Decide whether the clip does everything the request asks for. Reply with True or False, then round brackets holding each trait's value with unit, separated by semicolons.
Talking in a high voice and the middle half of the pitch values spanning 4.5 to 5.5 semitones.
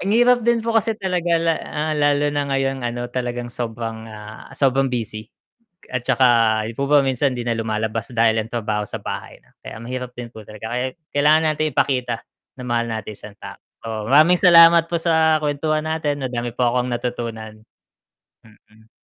False (125 Hz; 5.2 semitones)